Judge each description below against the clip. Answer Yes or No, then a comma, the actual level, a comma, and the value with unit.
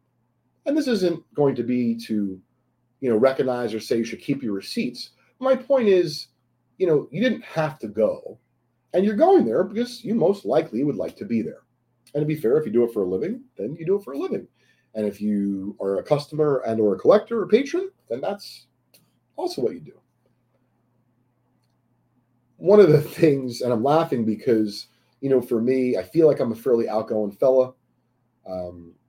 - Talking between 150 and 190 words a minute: No, average, 200 wpm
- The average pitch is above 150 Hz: No, low, 130 Hz